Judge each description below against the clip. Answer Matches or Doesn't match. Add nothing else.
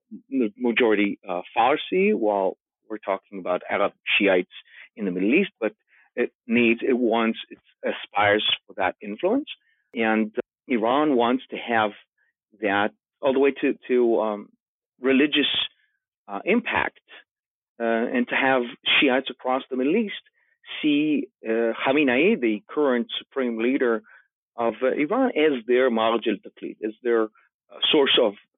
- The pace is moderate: Matches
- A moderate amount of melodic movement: Matches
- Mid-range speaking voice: Doesn't match